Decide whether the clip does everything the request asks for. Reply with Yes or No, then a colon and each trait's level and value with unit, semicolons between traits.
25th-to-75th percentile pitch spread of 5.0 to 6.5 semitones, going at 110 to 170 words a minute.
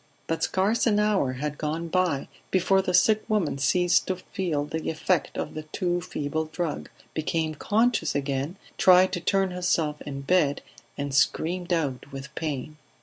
No: average, 3.8 semitones; average, 160 wpm